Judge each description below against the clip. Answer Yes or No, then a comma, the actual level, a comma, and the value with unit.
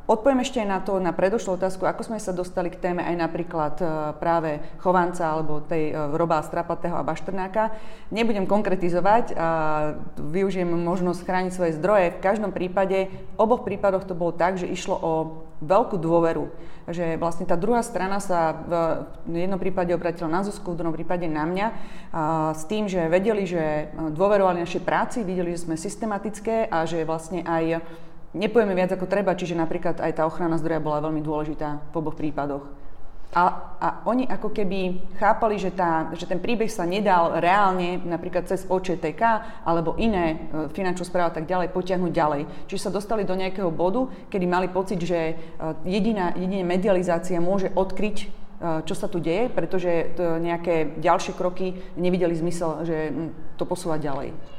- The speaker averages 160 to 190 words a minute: Yes, fast, 165 wpm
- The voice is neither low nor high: Yes, medium, 175 Hz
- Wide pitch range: No, average, 2.8 semitones